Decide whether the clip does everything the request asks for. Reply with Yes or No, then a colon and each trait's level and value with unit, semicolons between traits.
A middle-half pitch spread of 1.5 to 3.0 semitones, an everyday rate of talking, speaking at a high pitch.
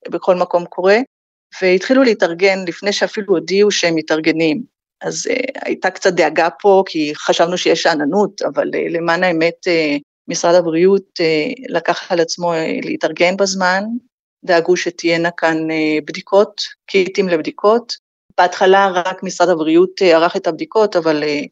No: average, 2.7 semitones; average, 140 wpm; medium, 180 Hz